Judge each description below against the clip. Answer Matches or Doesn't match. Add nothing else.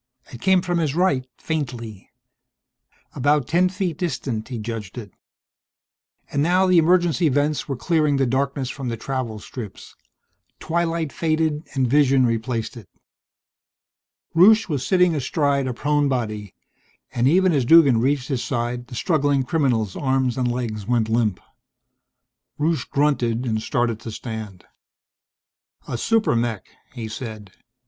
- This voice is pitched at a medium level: Doesn't match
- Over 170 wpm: Doesn't match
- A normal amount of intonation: Matches